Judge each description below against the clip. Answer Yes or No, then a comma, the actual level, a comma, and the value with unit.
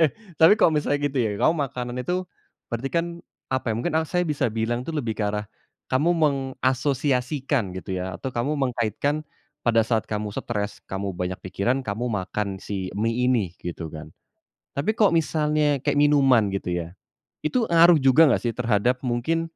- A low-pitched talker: Yes, low, 125 Hz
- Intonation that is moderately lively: No, wide, 5.8 semitones